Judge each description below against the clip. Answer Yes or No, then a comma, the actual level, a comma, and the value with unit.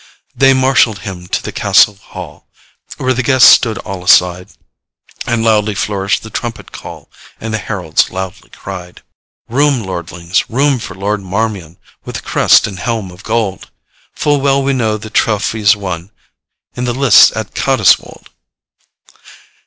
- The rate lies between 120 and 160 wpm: Yes, average, 150 wpm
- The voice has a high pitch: No, low, 105 Hz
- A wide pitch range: No, average, 4.2 semitones